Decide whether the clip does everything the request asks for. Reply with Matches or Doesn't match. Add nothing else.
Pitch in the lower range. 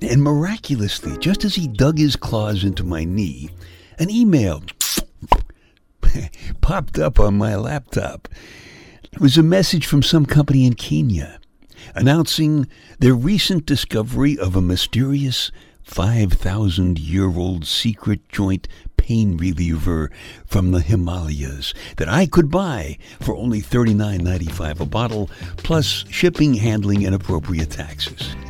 Matches